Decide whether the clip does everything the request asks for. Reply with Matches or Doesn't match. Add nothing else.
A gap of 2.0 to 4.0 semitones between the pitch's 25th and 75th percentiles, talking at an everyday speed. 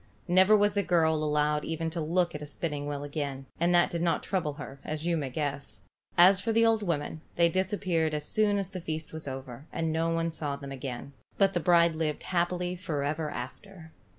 Doesn't match